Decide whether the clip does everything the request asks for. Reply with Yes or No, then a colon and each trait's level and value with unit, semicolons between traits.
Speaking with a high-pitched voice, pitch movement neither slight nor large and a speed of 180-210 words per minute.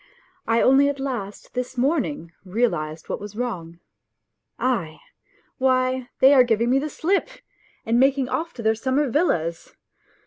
No: very high, 250 Hz; average, 4.6 semitones; average, 145 wpm